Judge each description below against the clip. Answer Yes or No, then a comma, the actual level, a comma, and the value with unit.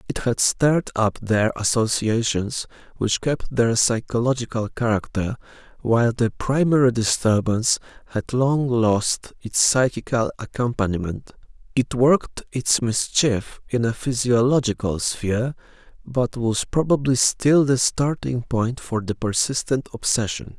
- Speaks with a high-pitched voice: No, low, 120 Hz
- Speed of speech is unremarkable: No, slow, 115 wpm